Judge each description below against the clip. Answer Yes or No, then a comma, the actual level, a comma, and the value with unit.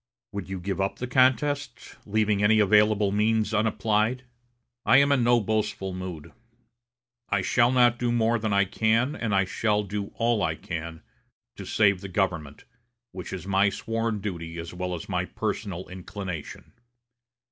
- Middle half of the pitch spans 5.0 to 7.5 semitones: No, average, 3.3 semitones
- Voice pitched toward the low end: Yes, low, 105 Hz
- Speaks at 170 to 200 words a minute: No, average, 160 wpm